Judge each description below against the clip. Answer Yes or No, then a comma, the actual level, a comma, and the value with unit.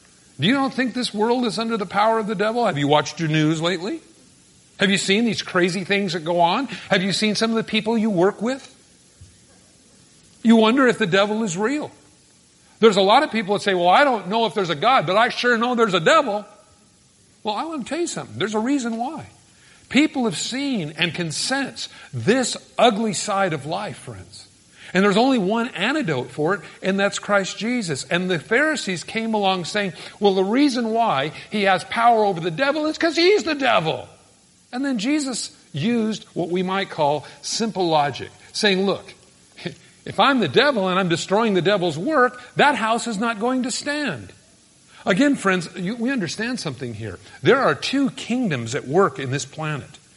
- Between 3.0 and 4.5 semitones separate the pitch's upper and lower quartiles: No, average, 4.9 semitones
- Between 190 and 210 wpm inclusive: Yes, average, 200 wpm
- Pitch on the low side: No, high, 210 Hz